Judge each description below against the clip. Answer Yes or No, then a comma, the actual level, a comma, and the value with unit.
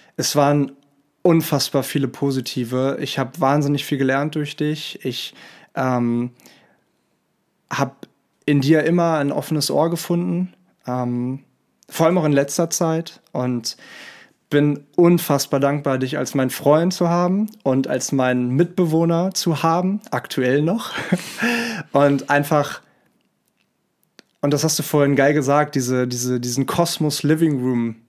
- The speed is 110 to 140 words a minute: Yes, average, 130 wpm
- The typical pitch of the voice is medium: Yes, medium, 145 Hz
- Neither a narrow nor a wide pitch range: Yes, average, 3.6 semitones